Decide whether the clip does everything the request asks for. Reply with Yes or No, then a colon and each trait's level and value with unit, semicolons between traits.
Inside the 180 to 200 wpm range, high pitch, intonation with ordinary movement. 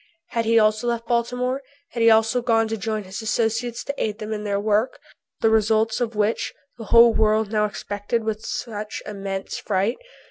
No: average, 185 wpm; high, 220 Hz; narrow, 1.6 semitones